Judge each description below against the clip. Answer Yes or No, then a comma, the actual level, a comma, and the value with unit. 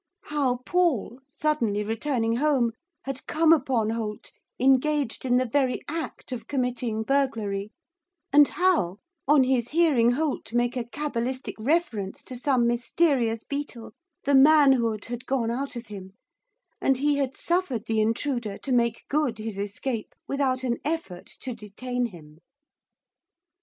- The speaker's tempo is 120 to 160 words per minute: Yes, average, 140 wpm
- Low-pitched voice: No, very high, 250 Hz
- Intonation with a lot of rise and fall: No, average, 3.9 semitones